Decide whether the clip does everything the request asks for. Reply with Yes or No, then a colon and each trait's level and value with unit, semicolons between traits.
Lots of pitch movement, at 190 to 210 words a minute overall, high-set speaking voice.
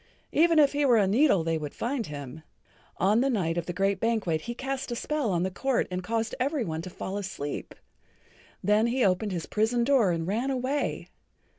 Yes: wide, 6.3 semitones; fast, 205 wpm; high, 215 Hz